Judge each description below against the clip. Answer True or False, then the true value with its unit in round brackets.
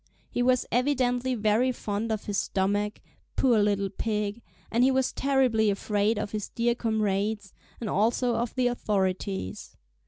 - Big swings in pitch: False (3.1 semitones)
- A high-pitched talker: True (220 Hz)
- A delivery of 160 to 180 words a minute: False (150 wpm)